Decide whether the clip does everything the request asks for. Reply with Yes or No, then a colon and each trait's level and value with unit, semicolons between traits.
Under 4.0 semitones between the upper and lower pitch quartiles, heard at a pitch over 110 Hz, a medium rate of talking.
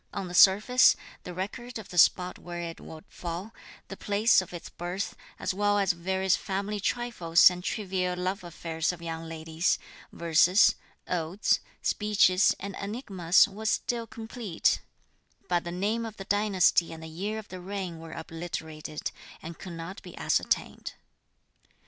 Yes: average, 3.2 semitones; medium, 185 Hz; average, 155 wpm